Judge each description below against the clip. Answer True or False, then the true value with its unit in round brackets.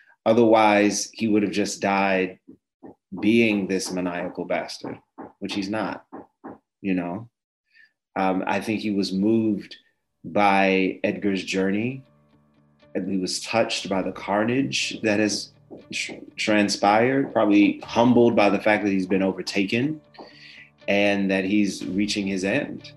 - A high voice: False (100 Hz)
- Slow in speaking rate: True (130 wpm)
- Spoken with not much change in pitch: True (2.2 semitones)